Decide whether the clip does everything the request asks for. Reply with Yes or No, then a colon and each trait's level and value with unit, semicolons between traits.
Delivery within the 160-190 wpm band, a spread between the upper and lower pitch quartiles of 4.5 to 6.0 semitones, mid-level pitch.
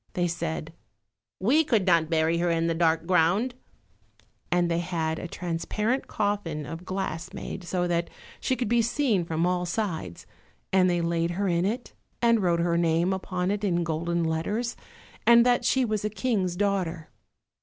No: average, 175 wpm; average, 3.7 semitones; medium, 175 Hz